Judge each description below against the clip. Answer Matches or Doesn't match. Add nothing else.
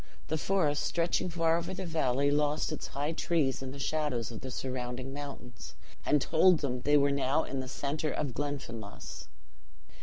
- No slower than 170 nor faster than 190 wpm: Matches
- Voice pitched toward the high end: Doesn't match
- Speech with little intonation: Doesn't match